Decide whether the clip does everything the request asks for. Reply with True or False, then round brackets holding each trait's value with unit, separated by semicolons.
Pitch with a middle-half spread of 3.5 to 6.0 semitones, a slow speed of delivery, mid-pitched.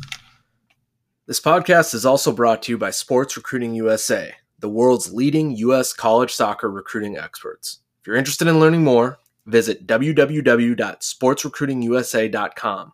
False (4.0 semitones; 125 wpm; 125 Hz)